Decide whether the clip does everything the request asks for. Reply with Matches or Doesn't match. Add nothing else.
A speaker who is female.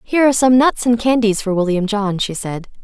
Matches